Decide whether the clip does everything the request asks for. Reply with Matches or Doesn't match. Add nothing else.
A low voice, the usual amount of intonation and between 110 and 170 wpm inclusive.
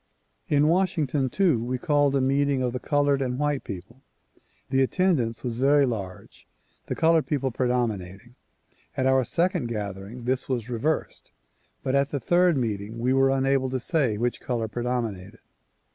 Matches